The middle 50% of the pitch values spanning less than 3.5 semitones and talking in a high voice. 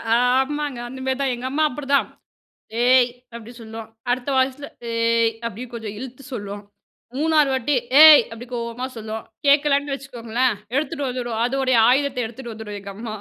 Yes: average, 3.1 semitones; very high, 250 Hz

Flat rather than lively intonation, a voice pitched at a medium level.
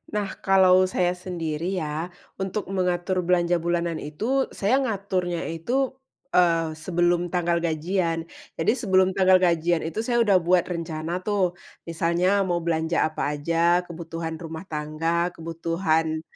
Yes: narrow, 2.2 semitones; medium, 175 Hz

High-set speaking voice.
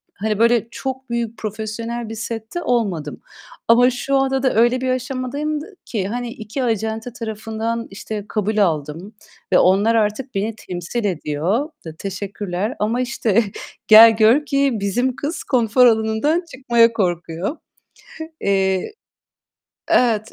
Yes: high, 225 Hz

